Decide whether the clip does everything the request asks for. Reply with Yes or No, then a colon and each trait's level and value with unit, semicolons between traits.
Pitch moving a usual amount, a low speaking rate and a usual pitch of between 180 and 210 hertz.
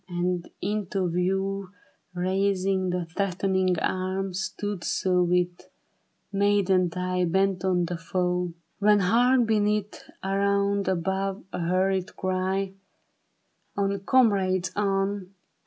No: narrow, 1.6 semitones; slow, 105 wpm; high, 190 Hz